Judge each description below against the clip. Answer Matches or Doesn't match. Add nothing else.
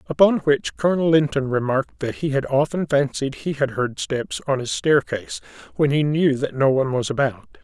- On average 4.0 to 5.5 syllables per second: Matches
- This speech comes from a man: Matches